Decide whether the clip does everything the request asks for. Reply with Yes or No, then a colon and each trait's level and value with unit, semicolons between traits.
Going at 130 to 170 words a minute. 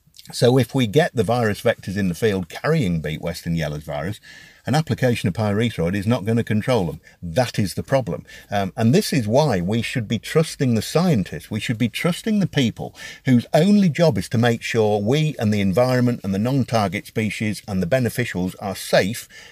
No: fast, 205 wpm